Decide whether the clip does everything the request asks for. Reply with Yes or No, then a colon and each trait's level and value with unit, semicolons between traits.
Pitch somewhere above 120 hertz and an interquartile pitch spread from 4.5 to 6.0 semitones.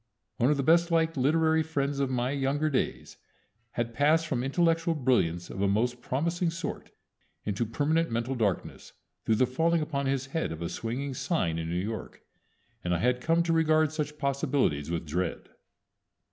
Yes: low, 135 Hz; wide, 5.6 semitones